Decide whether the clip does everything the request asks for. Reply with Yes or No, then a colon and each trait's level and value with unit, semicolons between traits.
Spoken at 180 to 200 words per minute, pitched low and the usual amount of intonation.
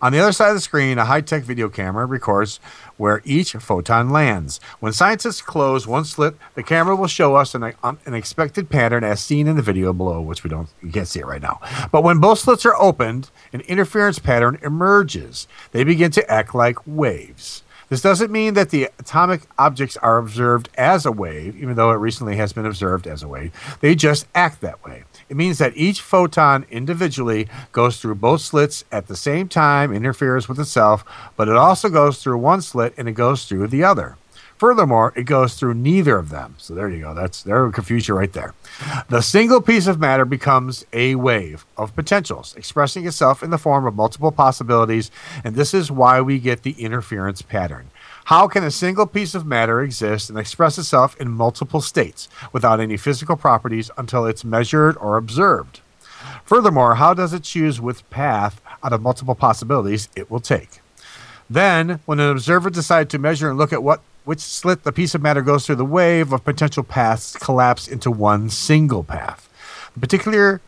No: average, 195 wpm; low, 130 Hz; wide, 5.8 semitones